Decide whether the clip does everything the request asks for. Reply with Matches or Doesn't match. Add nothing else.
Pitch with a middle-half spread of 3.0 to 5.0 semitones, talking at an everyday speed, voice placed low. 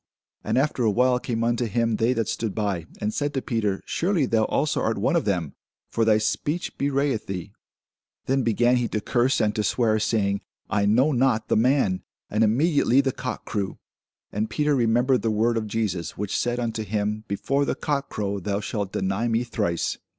Matches